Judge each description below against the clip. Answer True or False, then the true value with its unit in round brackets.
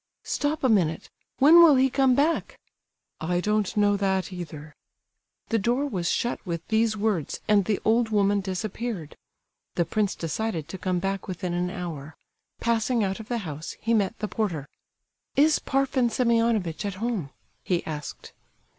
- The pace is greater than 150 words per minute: True (160 wpm)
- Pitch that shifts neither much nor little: True (4.7 semitones)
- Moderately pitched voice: False (205 Hz)